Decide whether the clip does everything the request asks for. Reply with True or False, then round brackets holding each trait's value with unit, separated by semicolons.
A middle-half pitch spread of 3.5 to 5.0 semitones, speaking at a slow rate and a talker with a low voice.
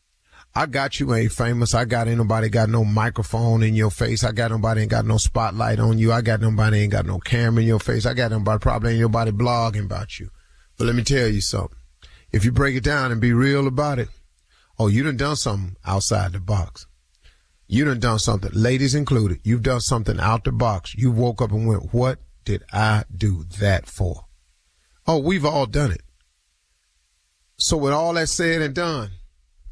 False (3.9 semitones; 205 wpm; 110 Hz)